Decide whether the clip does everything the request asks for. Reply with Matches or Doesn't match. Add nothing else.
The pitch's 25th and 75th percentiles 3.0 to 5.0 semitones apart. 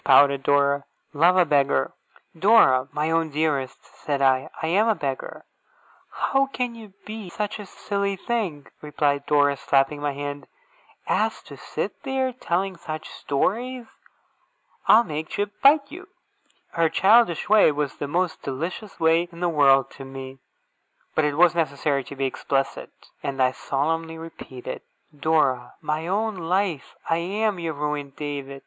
Doesn't match